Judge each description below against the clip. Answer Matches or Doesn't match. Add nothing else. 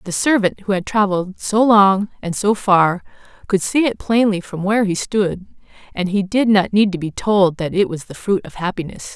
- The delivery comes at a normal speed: Doesn't match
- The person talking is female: Matches